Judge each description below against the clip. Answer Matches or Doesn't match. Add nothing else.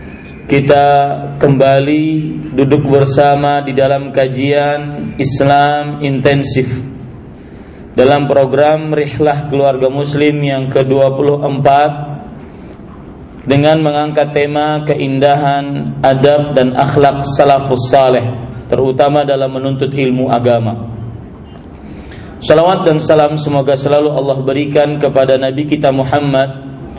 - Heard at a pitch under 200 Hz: Matches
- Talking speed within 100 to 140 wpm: Doesn't match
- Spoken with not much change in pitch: Matches